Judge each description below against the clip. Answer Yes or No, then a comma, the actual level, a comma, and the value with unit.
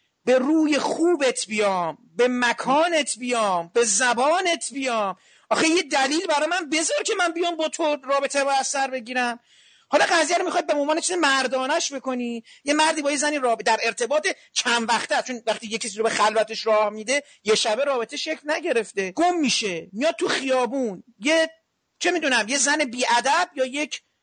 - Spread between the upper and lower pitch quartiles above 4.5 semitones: Yes, average, 5.1 semitones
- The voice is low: No, very high, 270 Hz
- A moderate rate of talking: No, fast, 170 wpm